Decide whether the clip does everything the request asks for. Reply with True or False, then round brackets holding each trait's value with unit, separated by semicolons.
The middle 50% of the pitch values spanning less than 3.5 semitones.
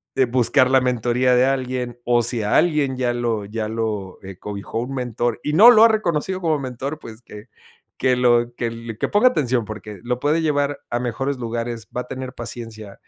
True (2.8 semitones)